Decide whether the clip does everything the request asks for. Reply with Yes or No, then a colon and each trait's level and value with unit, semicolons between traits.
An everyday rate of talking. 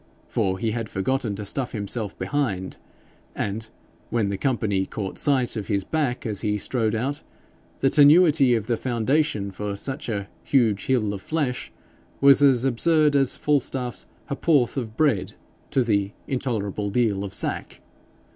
Yes: average, 150 wpm